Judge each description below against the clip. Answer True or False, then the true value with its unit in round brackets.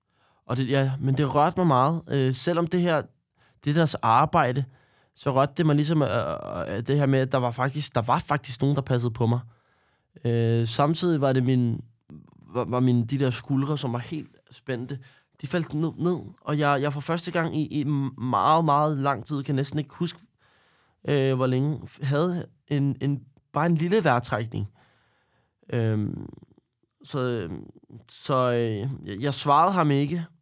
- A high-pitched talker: False (140 Hz)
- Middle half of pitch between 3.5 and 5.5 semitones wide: False (3.0 semitones)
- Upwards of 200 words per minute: False (175 wpm)